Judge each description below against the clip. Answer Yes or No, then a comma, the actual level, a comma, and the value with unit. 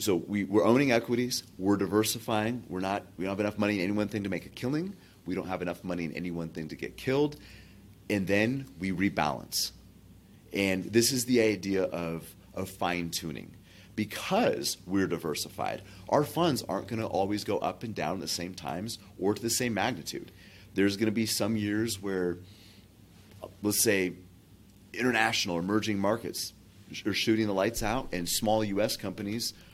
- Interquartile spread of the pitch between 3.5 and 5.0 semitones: No, average, 2.9 semitones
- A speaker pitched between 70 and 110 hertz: Yes, low, 100 Hz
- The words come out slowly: No, average, 180 wpm